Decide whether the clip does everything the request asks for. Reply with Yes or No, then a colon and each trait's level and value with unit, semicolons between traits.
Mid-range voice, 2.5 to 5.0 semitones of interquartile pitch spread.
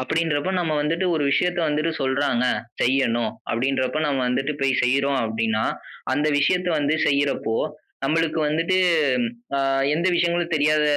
Yes: medium, 145 Hz; average, 3.7 semitones